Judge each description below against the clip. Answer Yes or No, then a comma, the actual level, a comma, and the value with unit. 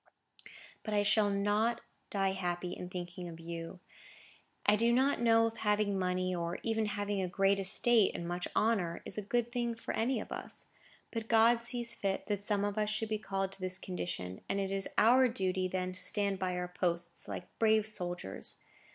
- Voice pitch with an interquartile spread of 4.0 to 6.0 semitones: No, average, 3.4 semitones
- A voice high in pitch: Yes, high, 200 Hz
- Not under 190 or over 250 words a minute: Yes, average, 195 wpm